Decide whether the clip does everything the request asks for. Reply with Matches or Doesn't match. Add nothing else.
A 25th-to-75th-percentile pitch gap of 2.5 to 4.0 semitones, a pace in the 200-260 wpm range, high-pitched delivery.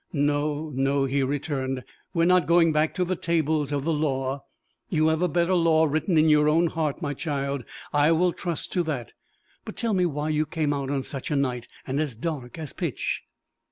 Doesn't match